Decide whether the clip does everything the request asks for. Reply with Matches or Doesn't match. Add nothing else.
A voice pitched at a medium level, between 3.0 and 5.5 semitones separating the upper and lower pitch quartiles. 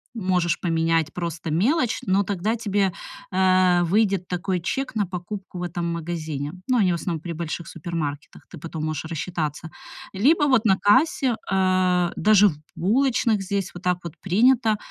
Matches